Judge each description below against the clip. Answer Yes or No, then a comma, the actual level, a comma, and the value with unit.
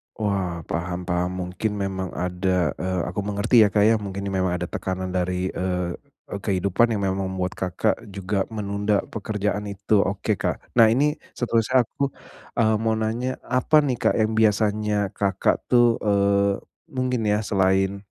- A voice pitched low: Yes, low, 100 Hz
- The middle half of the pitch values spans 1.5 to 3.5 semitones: Yes, average, 2.9 semitones